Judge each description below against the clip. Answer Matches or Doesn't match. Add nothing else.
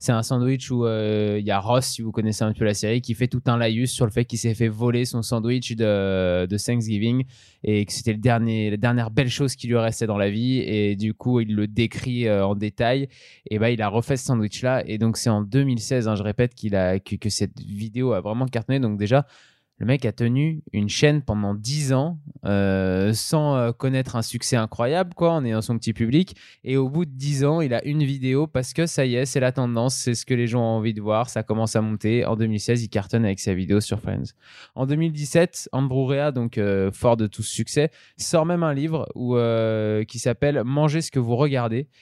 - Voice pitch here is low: Matches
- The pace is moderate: Doesn't match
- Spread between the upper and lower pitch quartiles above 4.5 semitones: Doesn't match